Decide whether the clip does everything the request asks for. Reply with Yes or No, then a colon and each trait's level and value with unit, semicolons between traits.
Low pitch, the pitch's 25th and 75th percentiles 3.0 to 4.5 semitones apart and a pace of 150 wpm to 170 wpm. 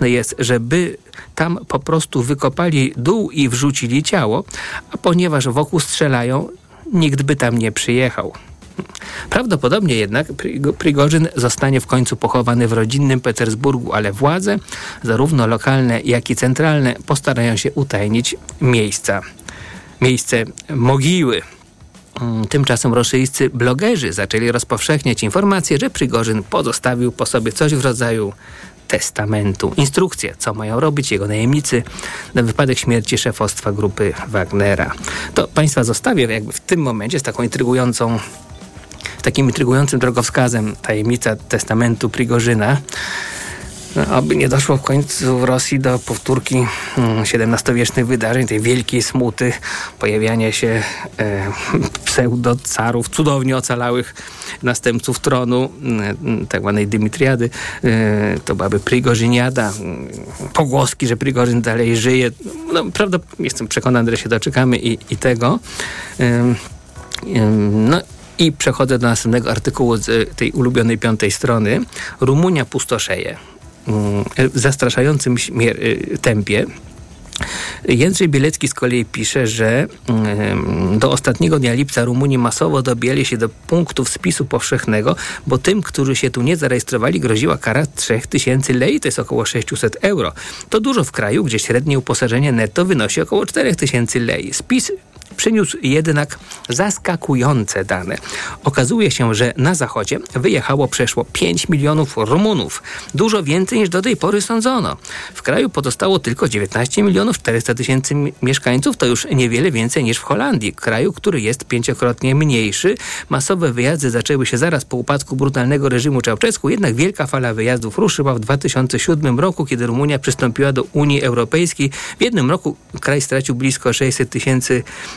No: low, 125 Hz; average, 3.3 semitones; average, 130 wpm